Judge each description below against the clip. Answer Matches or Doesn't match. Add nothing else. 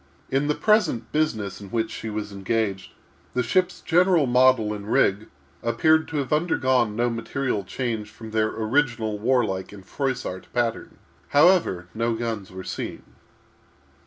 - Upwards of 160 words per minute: Doesn't match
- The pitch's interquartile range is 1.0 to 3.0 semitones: Doesn't match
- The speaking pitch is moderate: Doesn't match